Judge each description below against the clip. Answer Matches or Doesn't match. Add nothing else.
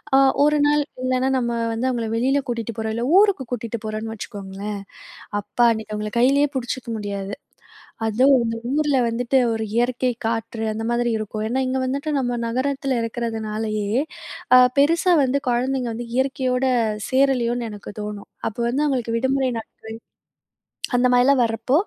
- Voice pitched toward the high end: Matches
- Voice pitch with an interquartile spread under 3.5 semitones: Matches